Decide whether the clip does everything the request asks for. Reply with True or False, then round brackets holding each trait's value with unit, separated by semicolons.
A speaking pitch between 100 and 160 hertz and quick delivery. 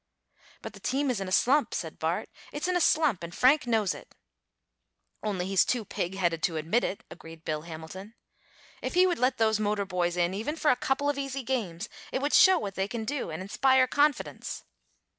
False (220 Hz; 210 wpm)